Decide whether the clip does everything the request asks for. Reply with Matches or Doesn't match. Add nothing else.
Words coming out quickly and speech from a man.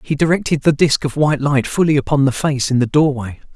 Matches